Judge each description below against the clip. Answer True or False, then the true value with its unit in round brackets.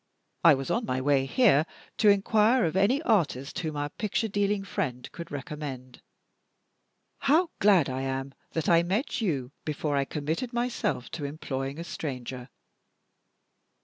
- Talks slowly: False (150 wpm)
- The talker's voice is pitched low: False (160 Hz)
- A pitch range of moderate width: False (7.3 semitones)